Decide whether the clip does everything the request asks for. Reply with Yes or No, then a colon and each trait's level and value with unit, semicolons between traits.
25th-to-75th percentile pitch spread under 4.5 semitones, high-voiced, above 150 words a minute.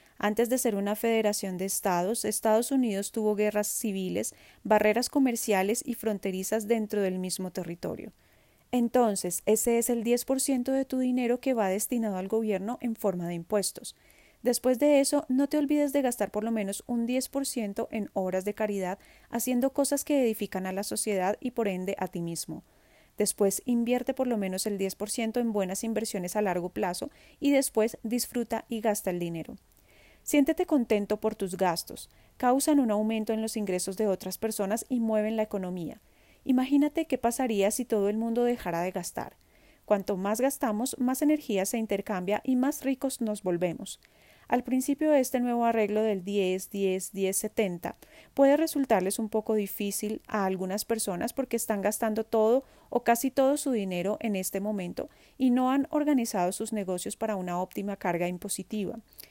Yes: average, 4.0 semitones; high, 220 Hz; average, 170 wpm